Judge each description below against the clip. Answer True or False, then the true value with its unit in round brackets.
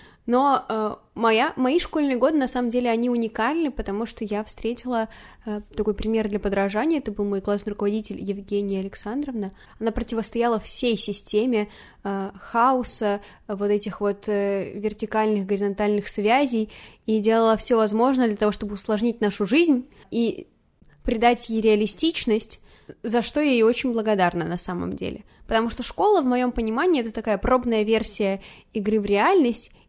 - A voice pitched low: False (220 Hz)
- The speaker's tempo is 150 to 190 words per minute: True (155 wpm)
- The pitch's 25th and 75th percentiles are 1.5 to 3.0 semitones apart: True (2.6 semitones)